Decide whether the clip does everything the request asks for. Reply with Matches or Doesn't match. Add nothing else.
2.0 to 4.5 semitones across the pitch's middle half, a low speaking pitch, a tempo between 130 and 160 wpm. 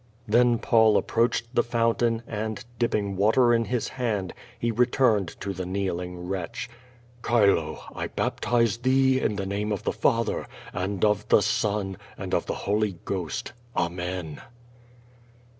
Matches